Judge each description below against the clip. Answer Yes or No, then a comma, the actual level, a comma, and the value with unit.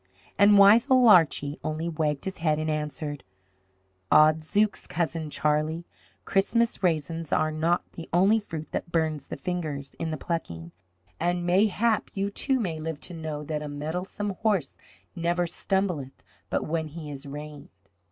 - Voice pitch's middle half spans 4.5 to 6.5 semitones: No, average, 3.4 semitones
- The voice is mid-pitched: Yes, medium, 160 Hz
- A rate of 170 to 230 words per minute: No, average, 155 wpm